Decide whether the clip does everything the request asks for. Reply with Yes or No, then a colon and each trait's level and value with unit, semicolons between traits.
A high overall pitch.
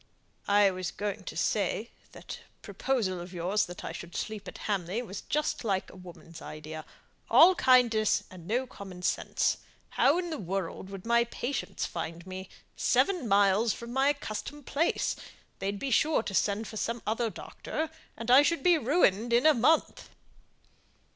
Yes: high, 215 Hz